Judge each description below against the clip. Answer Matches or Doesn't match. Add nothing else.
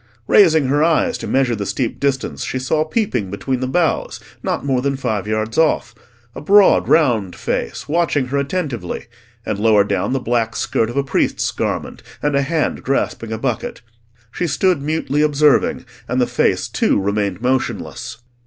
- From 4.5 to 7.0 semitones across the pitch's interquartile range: Matches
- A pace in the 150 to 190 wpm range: Matches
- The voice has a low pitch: Matches